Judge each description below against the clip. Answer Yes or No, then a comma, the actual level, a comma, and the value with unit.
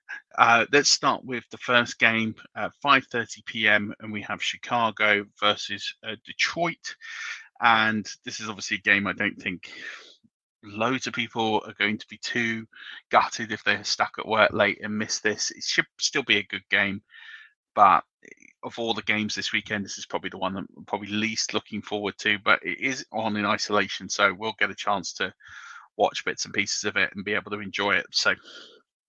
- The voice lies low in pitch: Yes, low, 110 Hz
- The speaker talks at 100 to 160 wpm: No, average, 195 wpm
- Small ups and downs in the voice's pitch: Yes, narrow, 2.2 semitones